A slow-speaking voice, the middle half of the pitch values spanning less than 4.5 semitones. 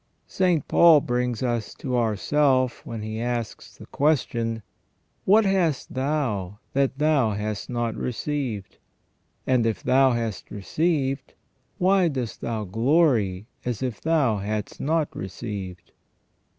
No: slow, 125 wpm; average, 5.2 semitones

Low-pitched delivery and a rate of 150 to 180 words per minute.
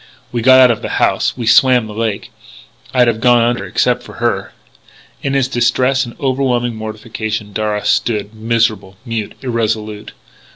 Yes: low, 115 Hz; average, 165 wpm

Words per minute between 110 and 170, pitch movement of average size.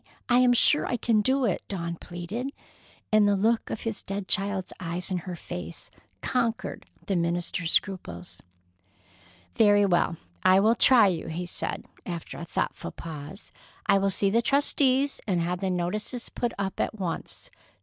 Yes: average, 165 wpm; average, 4.6 semitones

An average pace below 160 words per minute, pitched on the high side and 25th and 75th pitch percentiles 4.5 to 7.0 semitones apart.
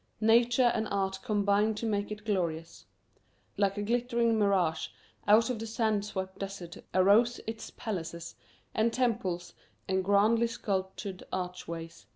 No: slow, 135 wpm; high, 205 Hz; average, 3.1 semitones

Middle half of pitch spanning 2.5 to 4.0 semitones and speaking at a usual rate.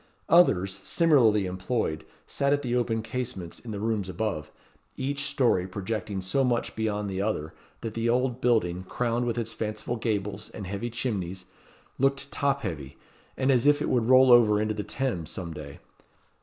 No: average, 4.6 semitones; average, 170 wpm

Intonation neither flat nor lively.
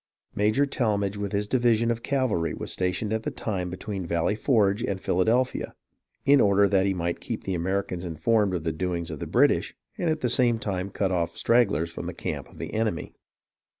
Yes: average, 4.0 semitones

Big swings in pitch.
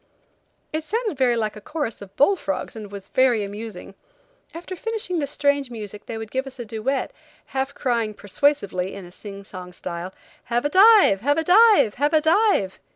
Yes: wide, 6.8 semitones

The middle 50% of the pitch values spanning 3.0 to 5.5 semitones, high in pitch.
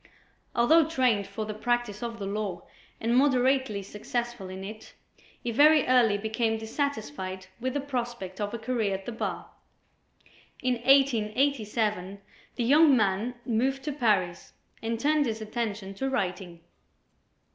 Yes: average, 3.9 semitones; high, 230 Hz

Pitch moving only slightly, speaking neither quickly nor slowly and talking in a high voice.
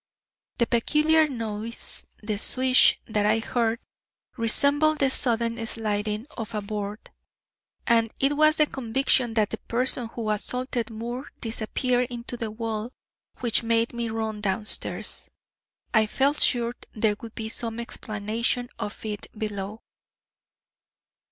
No: narrow, 2.3 semitones; slow, 130 wpm; high, 230 Hz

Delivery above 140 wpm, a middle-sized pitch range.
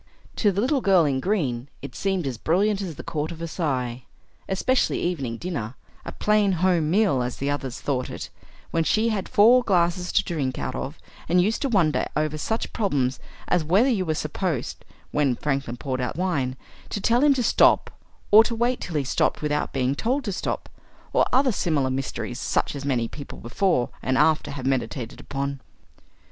No: average, 190 wpm; wide, 6.7 semitones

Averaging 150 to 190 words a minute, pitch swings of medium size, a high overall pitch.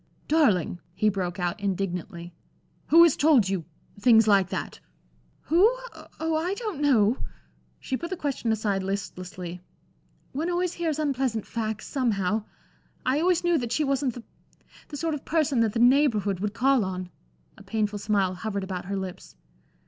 No: average, 160 wpm; wide, 7.1 semitones; high, 225 Hz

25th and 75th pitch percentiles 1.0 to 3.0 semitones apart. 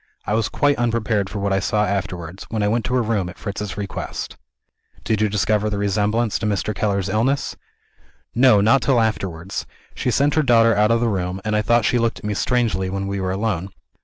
Yes: average, 2.7 semitones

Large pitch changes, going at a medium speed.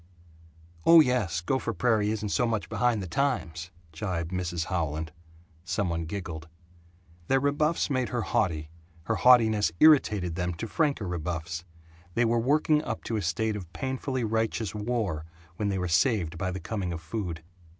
Yes: wide, 5.9 semitones; average, 160 wpm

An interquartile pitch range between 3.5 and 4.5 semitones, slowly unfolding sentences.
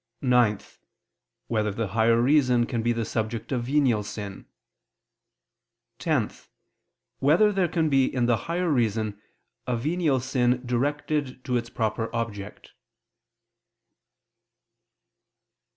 Yes: average, 3.8 semitones; slow, 110 wpm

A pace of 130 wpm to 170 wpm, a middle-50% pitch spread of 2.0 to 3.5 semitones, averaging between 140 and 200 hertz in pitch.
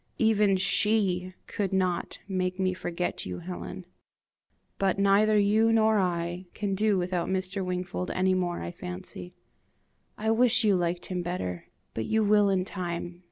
Yes: average, 155 wpm; narrow, 2.6 semitones; medium, 185 Hz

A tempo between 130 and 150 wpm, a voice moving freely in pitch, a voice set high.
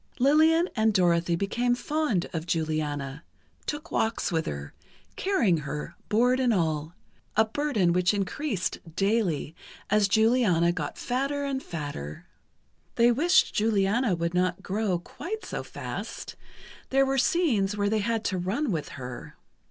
Yes: slow, 135 wpm; wide, 6.9 semitones; high, 205 Hz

